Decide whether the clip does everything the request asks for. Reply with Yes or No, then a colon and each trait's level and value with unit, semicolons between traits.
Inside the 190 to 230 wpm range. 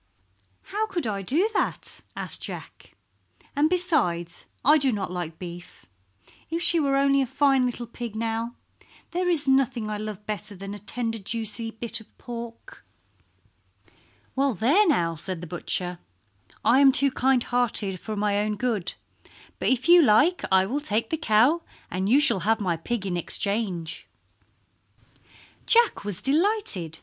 No: average, 160 wpm